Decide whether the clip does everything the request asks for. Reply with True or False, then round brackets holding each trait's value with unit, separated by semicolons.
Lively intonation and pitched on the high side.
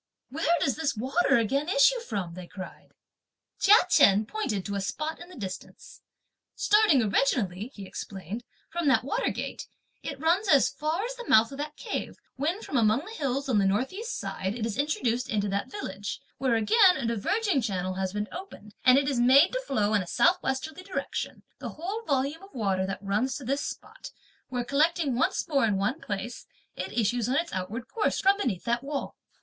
True (7.4 semitones; 260 Hz)